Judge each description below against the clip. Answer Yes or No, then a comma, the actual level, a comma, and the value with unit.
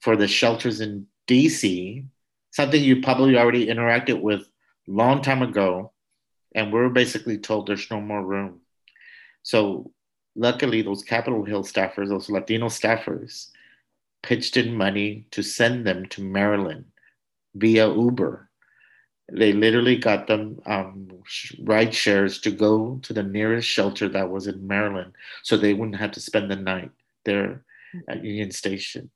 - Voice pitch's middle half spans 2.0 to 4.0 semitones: Yes, average, 2.8 semitones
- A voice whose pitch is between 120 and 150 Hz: No, low, 105 Hz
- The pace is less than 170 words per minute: Yes, average, 145 wpm